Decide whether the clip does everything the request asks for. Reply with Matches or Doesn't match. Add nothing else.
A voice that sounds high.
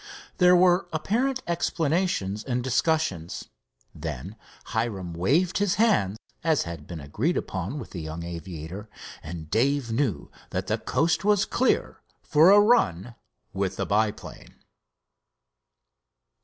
Doesn't match